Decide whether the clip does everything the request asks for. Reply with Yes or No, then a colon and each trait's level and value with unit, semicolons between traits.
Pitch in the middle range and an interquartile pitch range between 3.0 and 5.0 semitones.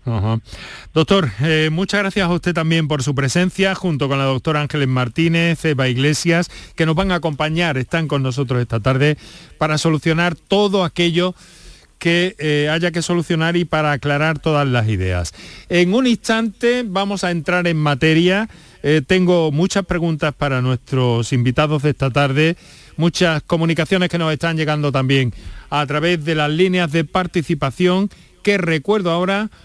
Yes: medium, 160 Hz; average, 3.5 semitones